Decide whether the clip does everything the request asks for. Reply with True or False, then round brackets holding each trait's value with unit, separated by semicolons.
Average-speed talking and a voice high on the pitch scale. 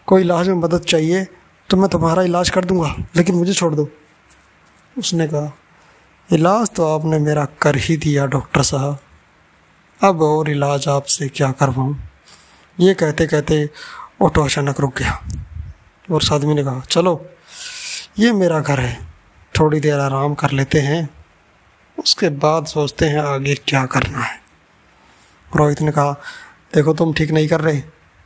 False (150 wpm; 150 Hz)